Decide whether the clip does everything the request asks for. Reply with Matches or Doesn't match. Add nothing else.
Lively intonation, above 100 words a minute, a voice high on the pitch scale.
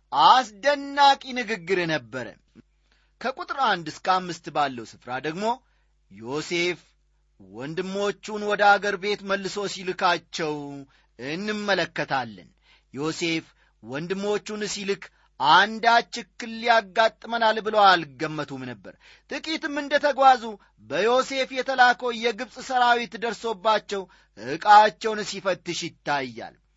Doesn't match